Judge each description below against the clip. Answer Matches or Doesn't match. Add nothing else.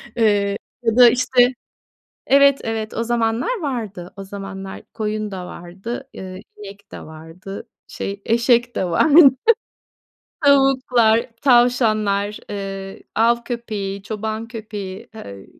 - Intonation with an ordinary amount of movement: Matches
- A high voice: Matches